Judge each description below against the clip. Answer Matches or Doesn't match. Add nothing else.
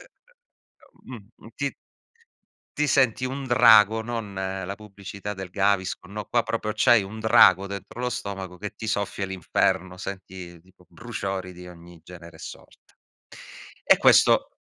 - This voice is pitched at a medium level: Doesn't match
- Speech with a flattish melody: Doesn't match